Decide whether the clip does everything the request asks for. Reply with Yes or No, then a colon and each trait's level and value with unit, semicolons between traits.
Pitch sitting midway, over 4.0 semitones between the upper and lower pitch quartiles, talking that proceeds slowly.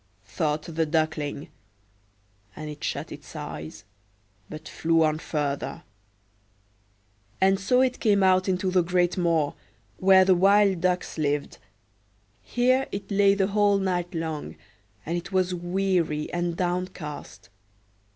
No: medium, 180 Hz; average, 3.5 semitones; slow, 130 wpm